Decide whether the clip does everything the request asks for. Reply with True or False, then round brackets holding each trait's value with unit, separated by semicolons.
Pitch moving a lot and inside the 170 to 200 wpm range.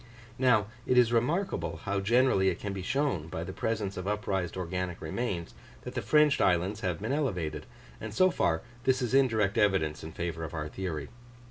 True (6.0 semitones; 190 wpm)